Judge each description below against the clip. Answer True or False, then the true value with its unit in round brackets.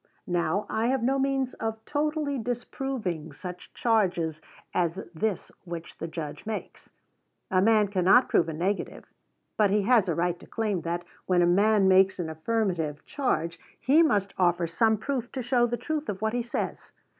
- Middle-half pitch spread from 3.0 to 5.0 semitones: False (5.6 semitones)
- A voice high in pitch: True (205 Hz)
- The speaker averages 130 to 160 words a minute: False (175 wpm)